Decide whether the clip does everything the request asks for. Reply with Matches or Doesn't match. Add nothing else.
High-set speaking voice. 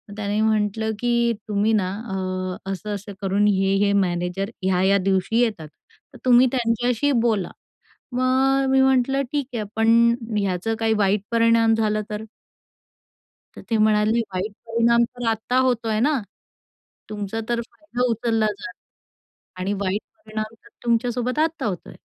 Matches